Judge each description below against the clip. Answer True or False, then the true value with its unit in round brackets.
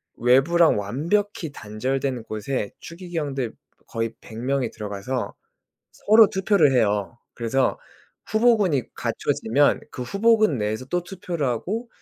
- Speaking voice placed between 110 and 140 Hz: True (135 Hz)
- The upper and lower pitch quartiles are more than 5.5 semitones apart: True (7.7 semitones)